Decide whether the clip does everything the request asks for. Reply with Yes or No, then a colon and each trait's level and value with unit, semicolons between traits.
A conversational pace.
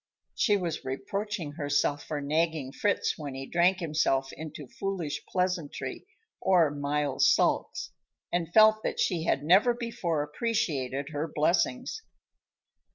No: slow, 125 wpm